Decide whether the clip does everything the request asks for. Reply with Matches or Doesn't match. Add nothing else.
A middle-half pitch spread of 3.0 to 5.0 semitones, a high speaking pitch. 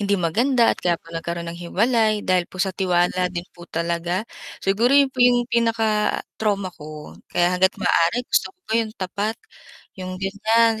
Matches